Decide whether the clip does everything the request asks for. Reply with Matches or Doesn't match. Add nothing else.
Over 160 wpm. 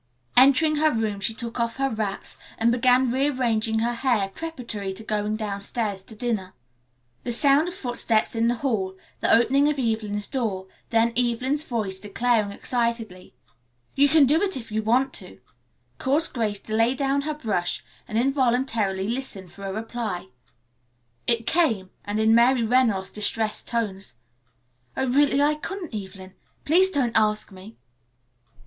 Doesn't match